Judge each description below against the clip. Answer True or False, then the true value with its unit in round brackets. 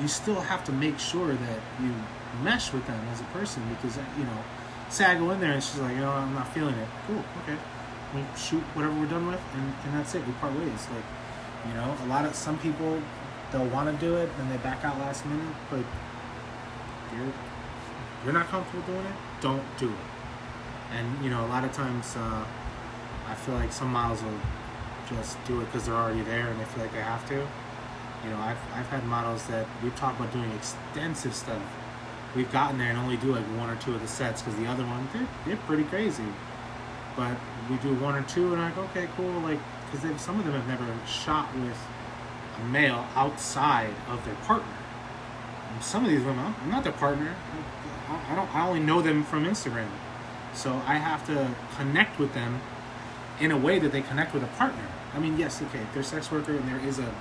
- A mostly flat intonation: False (3.5 semitones)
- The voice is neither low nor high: False (130 Hz)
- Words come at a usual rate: False (220 wpm)